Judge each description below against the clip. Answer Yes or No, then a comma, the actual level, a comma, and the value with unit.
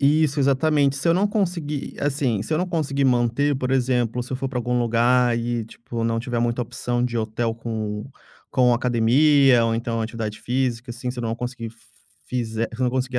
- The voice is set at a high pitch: No, low, 125 Hz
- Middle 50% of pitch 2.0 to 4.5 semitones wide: Yes, average, 2.8 semitones